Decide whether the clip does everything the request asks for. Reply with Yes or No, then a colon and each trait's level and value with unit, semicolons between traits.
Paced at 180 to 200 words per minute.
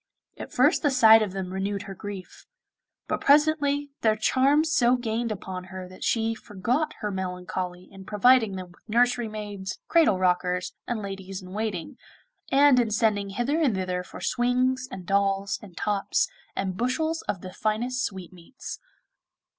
No: average, 160 wpm